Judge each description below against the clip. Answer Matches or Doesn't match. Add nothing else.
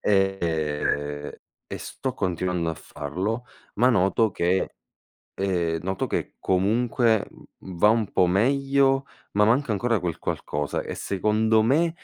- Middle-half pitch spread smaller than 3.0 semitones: Doesn't match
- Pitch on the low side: Matches